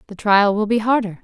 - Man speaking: No, female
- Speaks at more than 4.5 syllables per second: Yes, 5.8 syllables/s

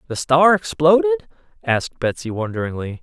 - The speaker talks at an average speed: No, slow, 120 wpm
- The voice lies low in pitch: Yes, low, 125 Hz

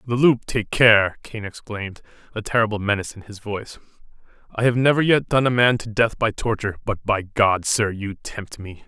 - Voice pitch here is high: No, low, 110 Hz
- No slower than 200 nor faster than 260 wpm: Yes, fast, 205 wpm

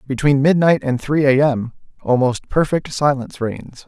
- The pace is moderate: Yes, average, 155 wpm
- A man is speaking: Yes, male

